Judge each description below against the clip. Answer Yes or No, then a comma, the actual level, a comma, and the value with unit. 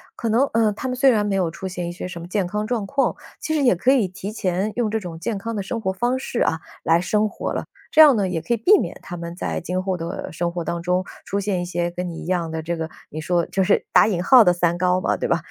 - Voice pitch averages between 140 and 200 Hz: Yes, medium, 185 Hz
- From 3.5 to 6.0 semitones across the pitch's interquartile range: Yes, average, 4.1 semitones